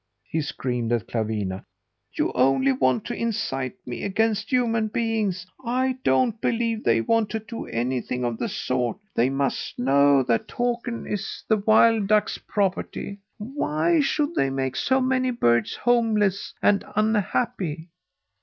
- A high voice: Yes, high, 200 Hz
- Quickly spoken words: No, average, 145 wpm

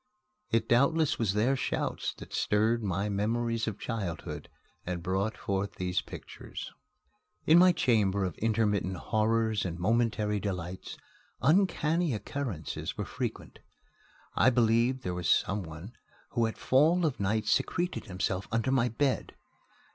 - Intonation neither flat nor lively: Yes, average, 4.4 semitones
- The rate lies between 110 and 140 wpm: Yes, slow, 135 wpm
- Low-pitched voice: Yes, low, 110 Hz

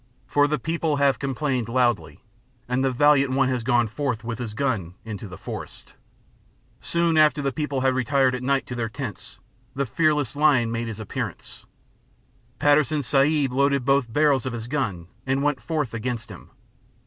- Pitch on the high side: No, low, 130 Hz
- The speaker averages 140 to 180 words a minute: Yes, average, 170 wpm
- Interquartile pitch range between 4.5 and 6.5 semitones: No, average, 3.4 semitones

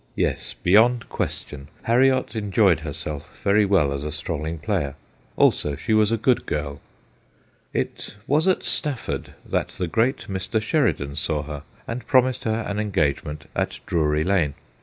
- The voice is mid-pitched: No, low, 100 Hz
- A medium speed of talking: Yes, average, 150 wpm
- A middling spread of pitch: No, wide, 7.3 semitones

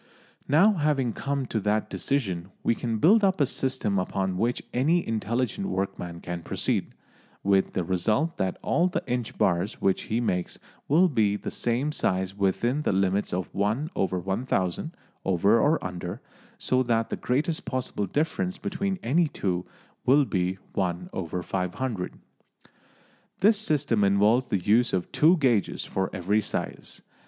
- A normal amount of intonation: No, wide, 6.9 semitones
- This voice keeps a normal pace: Yes, average, 145 wpm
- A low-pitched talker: Yes, low, 115 Hz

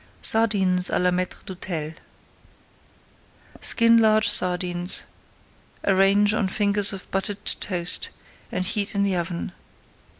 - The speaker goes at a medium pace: No, slow, 110 wpm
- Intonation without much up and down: Yes, narrow, 2.3 semitones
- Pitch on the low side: No, high, 195 Hz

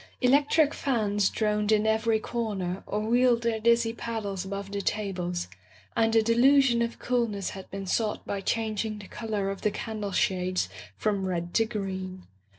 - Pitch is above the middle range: Yes, high, 215 Hz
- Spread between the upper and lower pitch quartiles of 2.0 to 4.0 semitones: Yes, average, 2.9 semitones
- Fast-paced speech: No, average, 160 wpm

